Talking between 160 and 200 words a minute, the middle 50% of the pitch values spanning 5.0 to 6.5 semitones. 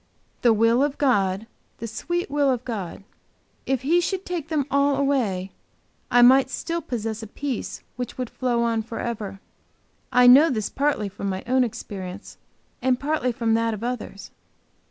No: average, 165 wpm; average, 4.1 semitones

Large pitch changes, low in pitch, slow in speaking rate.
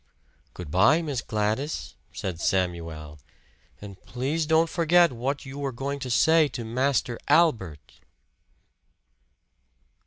Yes: wide, 7.6 semitones; low, 125 Hz; slow, 115 wpm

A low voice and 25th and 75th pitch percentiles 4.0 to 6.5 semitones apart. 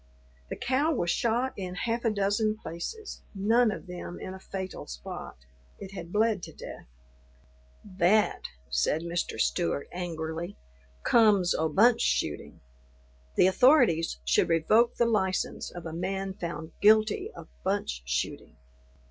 No: high, 190 Hz; average, 4.6 semitones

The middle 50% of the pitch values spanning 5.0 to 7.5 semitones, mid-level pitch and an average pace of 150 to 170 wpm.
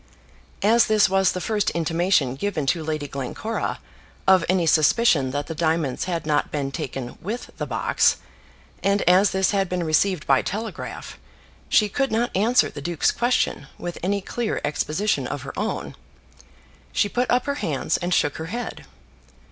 Yes: wide, 5.5 semitones; medium, 180 Hz; average, 165 wpm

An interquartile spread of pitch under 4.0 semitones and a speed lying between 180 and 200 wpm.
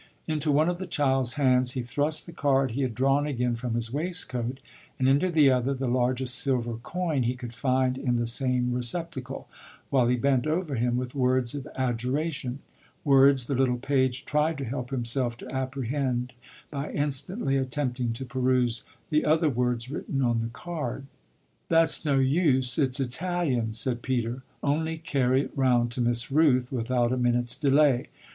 No: narrow, 2.6 semitones; average, 170 wpm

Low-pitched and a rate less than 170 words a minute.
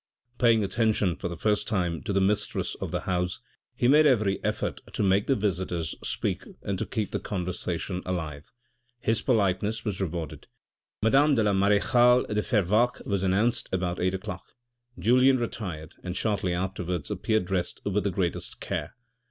Yes: low, 100 Hz; average, 160 wpm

